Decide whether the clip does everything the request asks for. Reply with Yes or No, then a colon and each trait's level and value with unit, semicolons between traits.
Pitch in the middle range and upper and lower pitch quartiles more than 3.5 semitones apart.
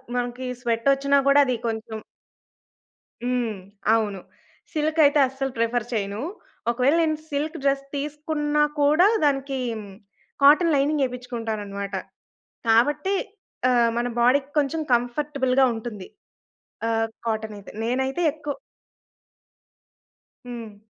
No: very high, 255 Hz; average, 4.0 semitones